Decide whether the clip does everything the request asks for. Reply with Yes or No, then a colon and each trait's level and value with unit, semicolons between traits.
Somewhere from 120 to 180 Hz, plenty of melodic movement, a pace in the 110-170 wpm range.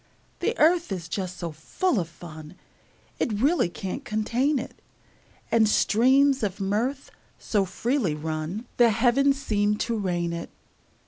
No: high, 215 Hz; wide, 6.7 semitones; average, 140 wpm